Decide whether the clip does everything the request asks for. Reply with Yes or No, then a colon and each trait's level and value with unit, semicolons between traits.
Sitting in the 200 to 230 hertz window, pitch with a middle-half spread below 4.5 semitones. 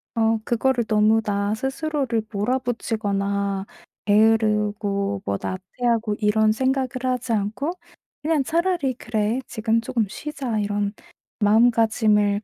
Yes: high, 220 Hz; average, 3.2 semitones